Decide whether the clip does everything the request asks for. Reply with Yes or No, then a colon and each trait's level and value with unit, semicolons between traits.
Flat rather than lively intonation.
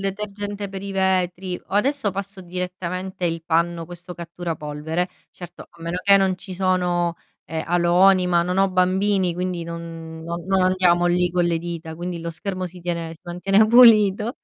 Yes: narrow, 2.0 semitones